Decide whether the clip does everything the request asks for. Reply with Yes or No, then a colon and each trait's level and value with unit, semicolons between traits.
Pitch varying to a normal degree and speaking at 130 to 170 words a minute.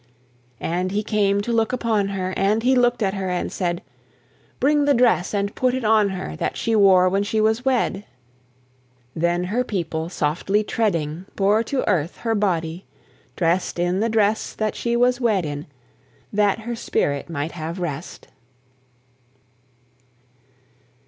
Yes: average, 4.2 semitones; average, 155 wpm